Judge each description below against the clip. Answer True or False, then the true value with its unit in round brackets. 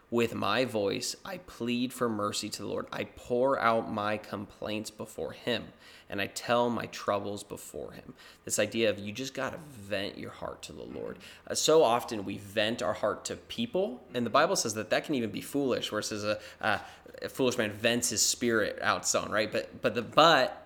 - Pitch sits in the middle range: False (110 Hz)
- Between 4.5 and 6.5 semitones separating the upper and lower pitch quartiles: False (2.7 semitones)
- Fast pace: True (215 wpm)